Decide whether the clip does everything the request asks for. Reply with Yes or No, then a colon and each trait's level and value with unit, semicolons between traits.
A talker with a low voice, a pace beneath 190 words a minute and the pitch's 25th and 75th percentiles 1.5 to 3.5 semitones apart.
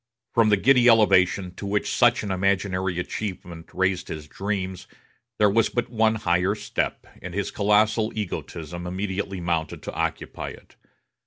Yes: low, 100 Hz; average, 150 wpm; average, 2.9 semitones